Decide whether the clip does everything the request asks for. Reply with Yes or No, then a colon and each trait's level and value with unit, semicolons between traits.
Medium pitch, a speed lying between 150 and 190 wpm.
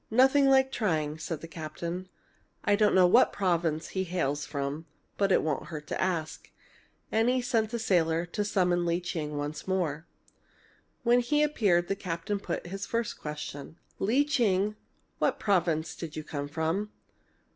Yes: medium, 175 Hz; average, 165 wpm